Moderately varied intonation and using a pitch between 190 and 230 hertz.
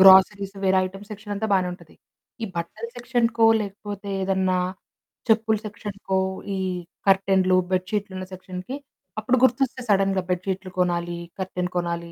No: narrow, 2.2 semitones; high, 195 Hz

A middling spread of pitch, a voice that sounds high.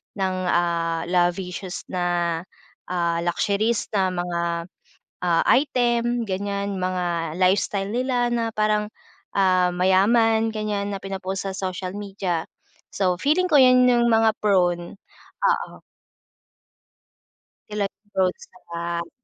Yes: average, 3.7 semitones; high, 195 Hz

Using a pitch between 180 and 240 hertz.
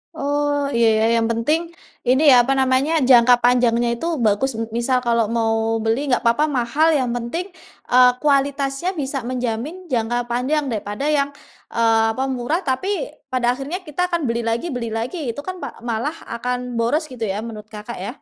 No: very high, 250 Hz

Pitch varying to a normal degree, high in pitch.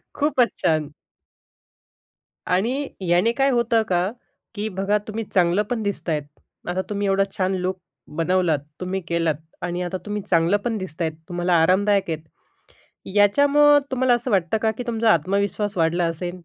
Yes: average, 4.1 semitones; high, 195 Hz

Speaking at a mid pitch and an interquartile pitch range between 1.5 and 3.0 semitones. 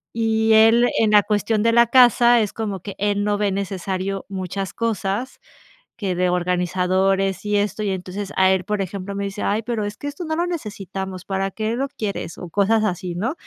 No: high, 205 Hz; narrow, 2.6 semitones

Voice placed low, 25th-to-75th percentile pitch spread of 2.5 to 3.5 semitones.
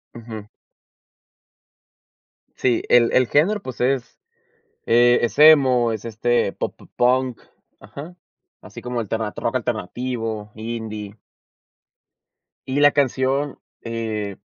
Yes: low, 120 Hz; average, 2.8 semitones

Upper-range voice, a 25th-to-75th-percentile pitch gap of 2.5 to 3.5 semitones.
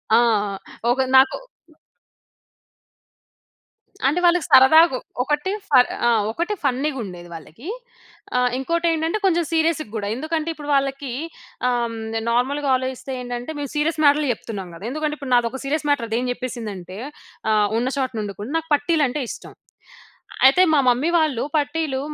No: very high, 270 Hz; average, 4.2 semitones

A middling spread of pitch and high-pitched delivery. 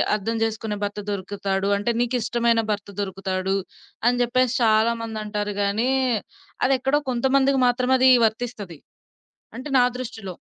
Yes: average, 3.5 semitones; high, 225 Hz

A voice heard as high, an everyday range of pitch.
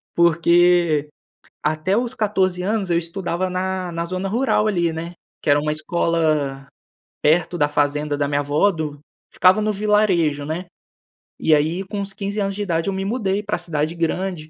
No: medium, 175 Hz; average, 4.0 semitones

